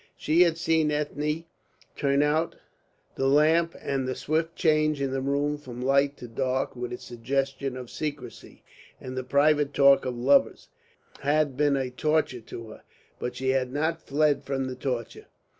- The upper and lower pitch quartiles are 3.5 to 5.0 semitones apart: No, average, 2.7 semitones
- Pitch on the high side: No, medium, 140 Hz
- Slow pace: No, average, 170 wpm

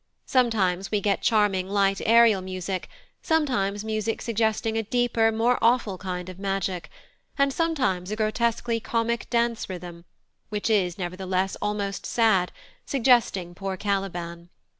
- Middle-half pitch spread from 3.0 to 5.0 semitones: Yes, average, 3.6 semitones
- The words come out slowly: Yes, slow, 130 wpm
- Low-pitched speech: No, high, 205 Hz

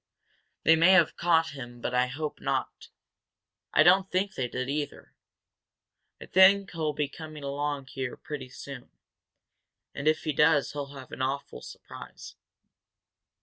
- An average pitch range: Yes, average, 3.6 semitones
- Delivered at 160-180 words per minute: No, average, 145 wpm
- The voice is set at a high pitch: No, medium, 145 Hz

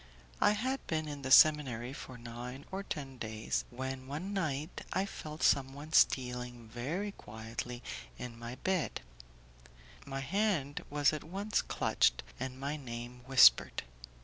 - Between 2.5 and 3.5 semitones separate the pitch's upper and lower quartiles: No, average, 4.2 semitones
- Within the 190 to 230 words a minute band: No, average, 140 wpm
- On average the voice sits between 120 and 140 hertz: Yes, low, 135 Hz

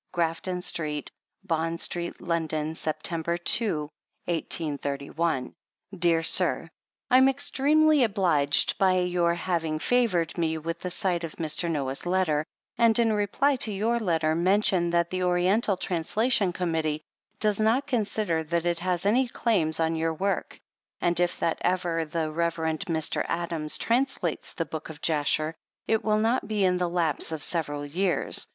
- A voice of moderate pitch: Yes, medium, 170 Hz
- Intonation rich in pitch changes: No, average, 3.7 semitones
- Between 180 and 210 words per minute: No, average, 150 wpm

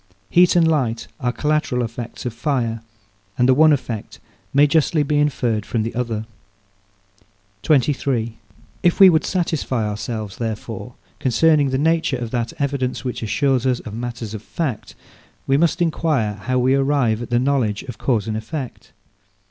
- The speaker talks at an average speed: Yes, average, 160 wpm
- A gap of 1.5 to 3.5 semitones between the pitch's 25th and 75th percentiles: No, average, 4.4 semitones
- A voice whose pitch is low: Yes, low, 125 Hz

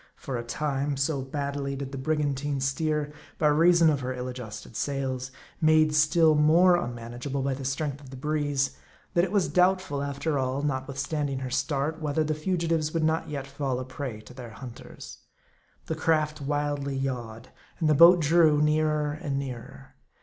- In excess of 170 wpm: Yes, average, 180 wpm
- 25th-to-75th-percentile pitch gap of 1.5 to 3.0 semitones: Yes, narrow, 2.6 semitones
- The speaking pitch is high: No, medium, 145 Hz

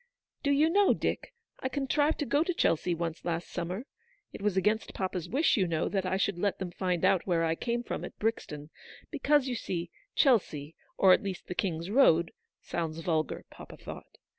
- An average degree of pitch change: No, wide, 6.5 semitones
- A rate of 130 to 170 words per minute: No, average, 195 wpm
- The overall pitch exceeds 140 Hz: Yes, high, 190 Hz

